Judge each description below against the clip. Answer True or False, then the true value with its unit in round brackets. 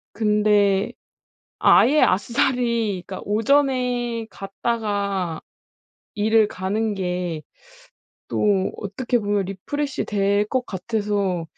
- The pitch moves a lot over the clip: False (3.1 semitones)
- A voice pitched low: False (210 Hz)